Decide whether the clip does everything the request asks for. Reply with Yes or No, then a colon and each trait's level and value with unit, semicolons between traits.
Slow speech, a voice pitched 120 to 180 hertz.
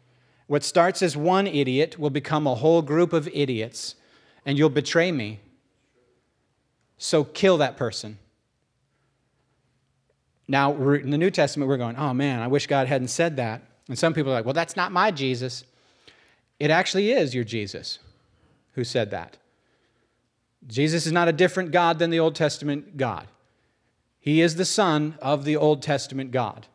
No: average, 165 wpm; medium, 140 Hz